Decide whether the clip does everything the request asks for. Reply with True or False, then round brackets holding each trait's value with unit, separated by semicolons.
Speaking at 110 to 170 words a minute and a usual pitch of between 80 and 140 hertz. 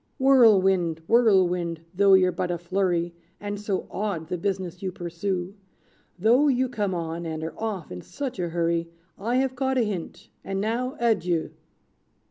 False (160 wpm; 190 Hz)